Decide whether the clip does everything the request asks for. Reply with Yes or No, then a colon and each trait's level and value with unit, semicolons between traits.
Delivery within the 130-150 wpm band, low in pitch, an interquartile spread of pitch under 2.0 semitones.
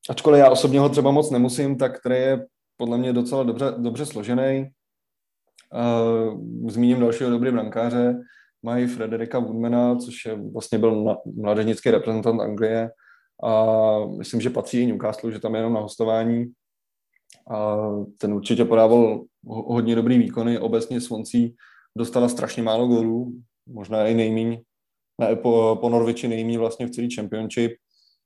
Yes: average, 140 wpm; low, 115 Hz; narrow, 1.5 semitones